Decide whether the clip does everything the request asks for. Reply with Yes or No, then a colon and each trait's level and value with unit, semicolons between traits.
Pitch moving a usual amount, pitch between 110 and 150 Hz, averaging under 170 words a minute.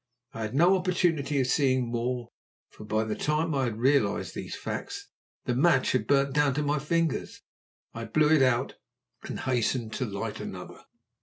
No: average, 4.0 semitones; low, 135 Hz; average, 175 wpm